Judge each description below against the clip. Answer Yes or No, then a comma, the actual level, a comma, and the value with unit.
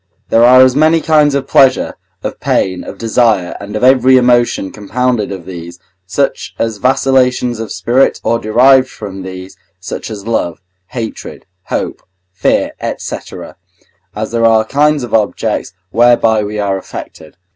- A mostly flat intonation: No, average, 4.0 semitones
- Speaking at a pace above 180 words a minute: No, average, 150 wpm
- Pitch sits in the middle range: No, low, 115 Hz